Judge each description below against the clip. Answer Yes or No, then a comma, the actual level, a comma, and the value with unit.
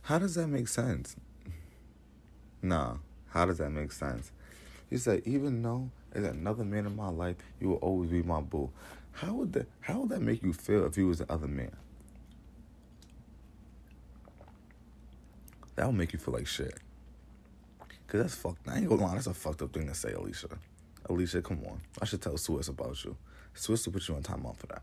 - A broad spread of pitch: Yes, wide, 6.0 semitones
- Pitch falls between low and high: No, very low, 85 Hz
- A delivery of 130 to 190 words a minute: No, average, 200 wpm